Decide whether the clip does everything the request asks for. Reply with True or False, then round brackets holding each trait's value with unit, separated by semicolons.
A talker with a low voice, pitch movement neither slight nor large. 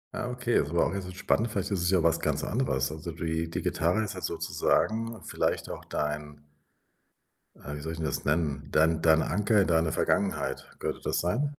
True (85 Hz; 4.2 semitones)